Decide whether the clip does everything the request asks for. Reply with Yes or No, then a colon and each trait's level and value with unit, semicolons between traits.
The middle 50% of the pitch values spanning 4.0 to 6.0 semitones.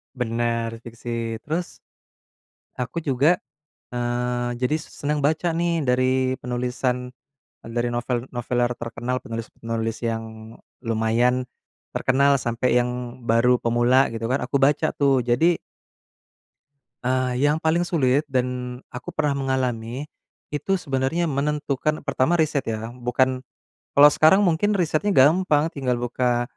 No: average, 3.4 semitones